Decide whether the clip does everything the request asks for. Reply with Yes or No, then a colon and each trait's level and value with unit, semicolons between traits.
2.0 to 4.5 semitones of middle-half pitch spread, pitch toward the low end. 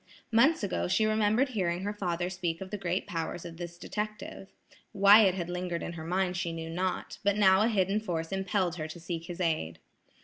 No: average, 2.9 semitones; medium, 185 Hz